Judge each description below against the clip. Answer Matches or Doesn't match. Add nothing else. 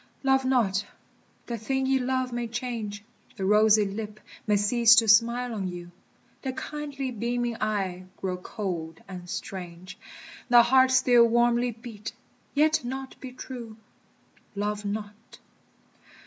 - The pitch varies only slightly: Doesn't match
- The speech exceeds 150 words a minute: Doesn't match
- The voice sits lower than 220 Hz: Doesn't match